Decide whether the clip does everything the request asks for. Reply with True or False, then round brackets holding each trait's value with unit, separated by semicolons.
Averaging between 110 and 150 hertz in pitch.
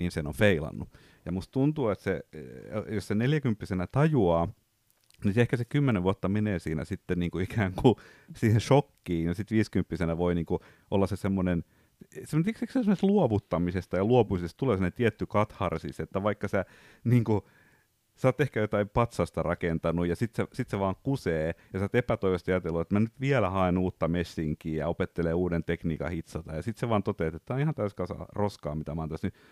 False (100 Hz)